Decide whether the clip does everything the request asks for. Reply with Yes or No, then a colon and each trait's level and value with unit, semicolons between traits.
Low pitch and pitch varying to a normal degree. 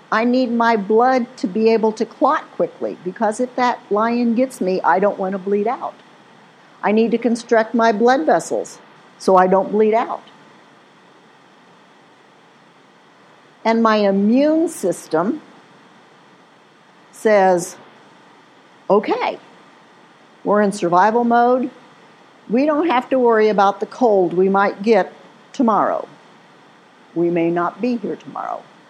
No: high, 225 Hz; average, 3.5 semitones